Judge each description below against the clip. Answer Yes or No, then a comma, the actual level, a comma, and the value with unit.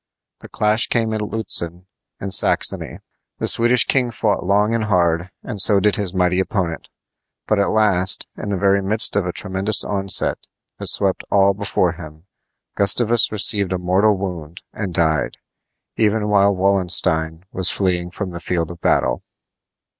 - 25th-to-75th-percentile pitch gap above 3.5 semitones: No, average, 2.9 semitones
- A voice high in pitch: No, very low, 95 Hz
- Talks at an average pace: Yes, average, 160 wpm